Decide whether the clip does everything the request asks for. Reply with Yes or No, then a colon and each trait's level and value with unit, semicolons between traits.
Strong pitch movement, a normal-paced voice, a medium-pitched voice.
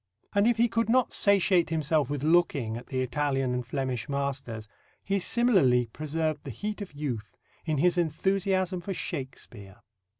Yes: wide, 6.5 semitones; average, 160 wpm; medium, 150 Hz